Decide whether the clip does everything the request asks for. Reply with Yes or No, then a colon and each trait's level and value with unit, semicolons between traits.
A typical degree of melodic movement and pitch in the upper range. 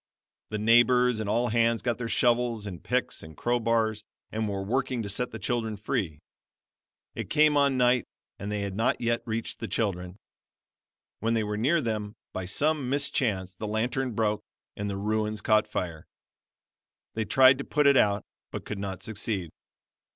No: average, 3.1 semitones; low, 110 Hz